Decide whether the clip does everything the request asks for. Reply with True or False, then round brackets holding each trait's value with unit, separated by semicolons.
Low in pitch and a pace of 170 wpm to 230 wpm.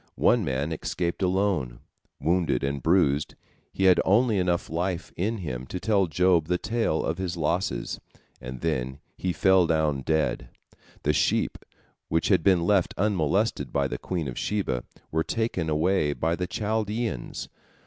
False (85 Hz; 155 wpm)